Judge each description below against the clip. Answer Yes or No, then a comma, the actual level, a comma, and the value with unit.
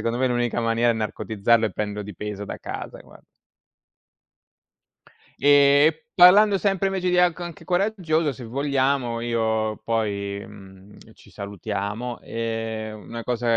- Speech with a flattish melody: No, average, 5.2 semitones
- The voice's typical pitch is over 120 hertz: No, low, 115 Hz